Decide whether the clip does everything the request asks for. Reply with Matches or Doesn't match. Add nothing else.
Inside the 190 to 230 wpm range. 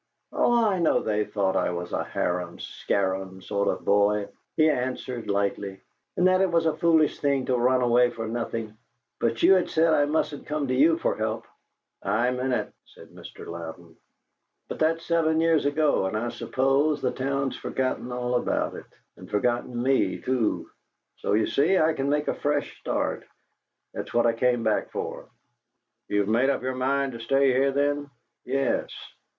Doesn't match